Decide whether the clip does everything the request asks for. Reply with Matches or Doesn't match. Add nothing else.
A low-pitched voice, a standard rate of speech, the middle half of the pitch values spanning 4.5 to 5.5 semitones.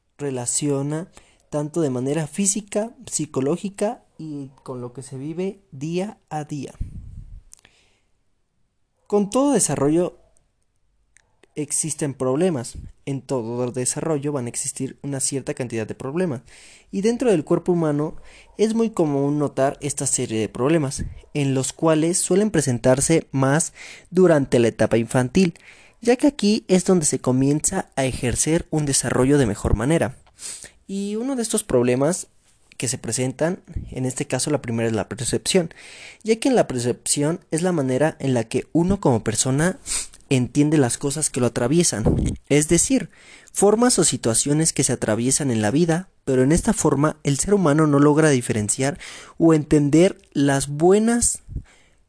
Doesn't match